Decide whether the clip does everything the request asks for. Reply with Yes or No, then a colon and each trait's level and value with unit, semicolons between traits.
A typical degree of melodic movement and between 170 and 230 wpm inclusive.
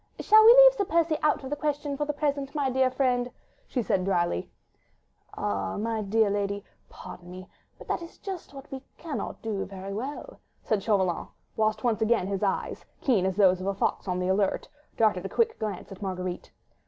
No: wide, 6.8 semitones; average, 200 wpm